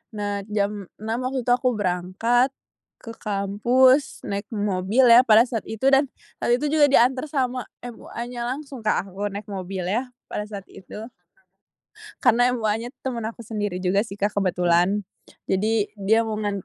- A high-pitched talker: Yes, high, 220 Hz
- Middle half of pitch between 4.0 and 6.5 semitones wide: No, average, 3.5 semitones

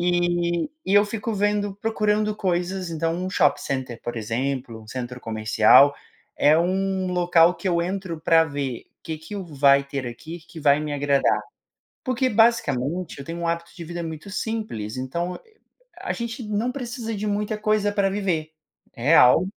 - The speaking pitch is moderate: Yes, medium, 170 Hz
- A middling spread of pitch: No, wide, 6.2 semitones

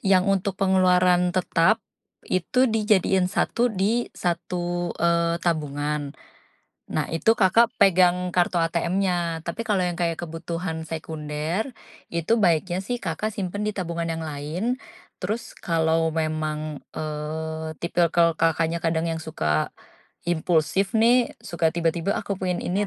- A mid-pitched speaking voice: Yes, medium, 175 Hz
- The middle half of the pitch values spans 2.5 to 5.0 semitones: Yes, average, 2.9 semitones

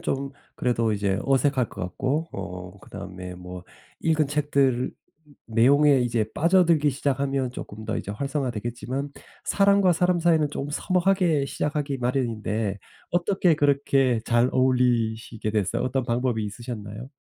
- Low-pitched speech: Yes, low, 130 Hz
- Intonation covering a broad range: No, average, 4.8 semitones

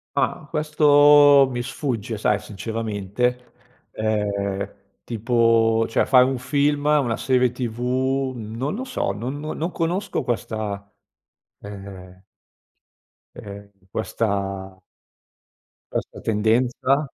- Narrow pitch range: No, average, 4.6 semitones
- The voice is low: Yes, low, 120 Hz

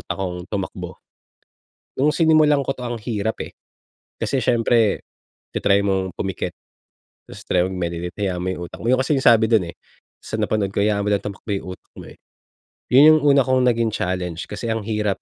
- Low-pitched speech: Yes, low, 105 Hz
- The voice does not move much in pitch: No, average, 4.6 semitones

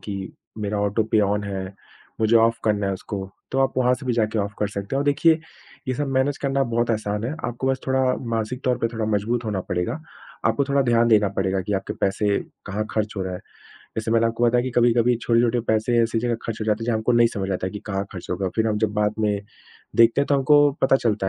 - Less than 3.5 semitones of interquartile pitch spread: Yes, average, 2.9 semitones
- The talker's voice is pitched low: Yes, low, 110 Hz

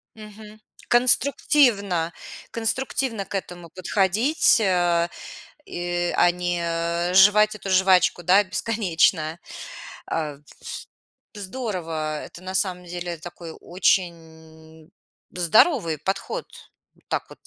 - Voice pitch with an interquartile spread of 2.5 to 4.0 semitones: Yes, average, 3.6 semitones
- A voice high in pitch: No, medium, 180 Hz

